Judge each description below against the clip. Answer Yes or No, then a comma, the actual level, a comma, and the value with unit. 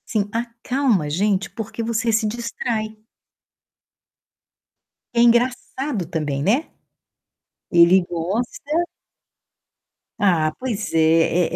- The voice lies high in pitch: Yes, high, 215 Hz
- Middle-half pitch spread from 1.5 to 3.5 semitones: No, wide, 5.4 semitones